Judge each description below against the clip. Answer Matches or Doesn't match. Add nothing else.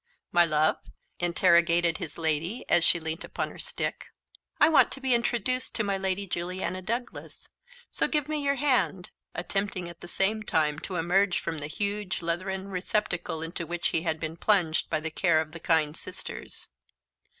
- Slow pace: Doesn't match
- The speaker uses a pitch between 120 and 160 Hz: Doesn't match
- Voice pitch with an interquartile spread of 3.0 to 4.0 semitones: Matches